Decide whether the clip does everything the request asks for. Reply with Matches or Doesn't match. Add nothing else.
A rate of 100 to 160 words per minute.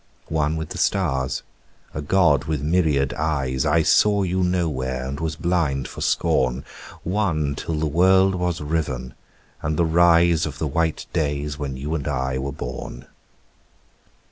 Matches